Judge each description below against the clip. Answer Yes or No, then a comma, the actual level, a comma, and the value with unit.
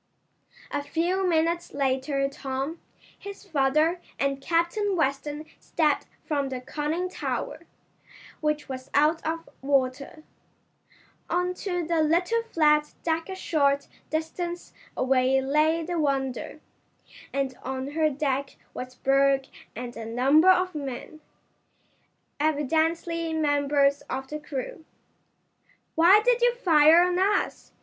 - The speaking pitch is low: No, very high, 300 Hz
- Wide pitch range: No, average, 3.6 semitones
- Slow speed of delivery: Yes, slow, 120 wpm